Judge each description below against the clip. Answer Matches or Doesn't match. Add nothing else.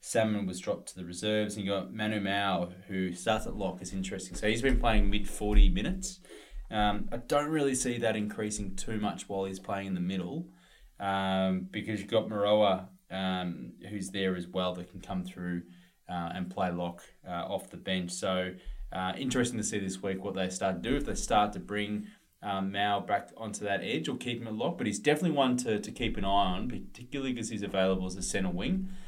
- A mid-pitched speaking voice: Doesn't match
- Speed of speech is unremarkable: Doesn't match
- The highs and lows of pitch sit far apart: Doesn't match